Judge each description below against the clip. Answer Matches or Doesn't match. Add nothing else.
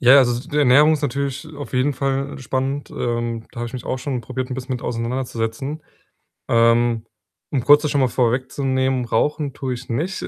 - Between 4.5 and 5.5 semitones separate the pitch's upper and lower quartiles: Doesn't match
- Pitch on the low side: Matches